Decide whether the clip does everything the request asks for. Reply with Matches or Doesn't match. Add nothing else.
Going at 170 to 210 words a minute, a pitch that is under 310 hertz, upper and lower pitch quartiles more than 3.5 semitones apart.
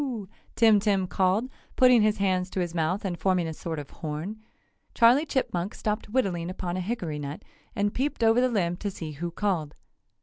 Matches